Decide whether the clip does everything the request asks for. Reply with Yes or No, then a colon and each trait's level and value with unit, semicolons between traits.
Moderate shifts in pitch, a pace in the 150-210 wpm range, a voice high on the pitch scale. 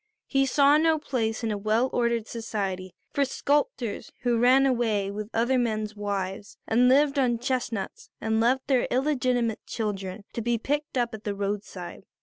Yes: average, 3.6 semitones; average, 165 wpm; high, 235 Hz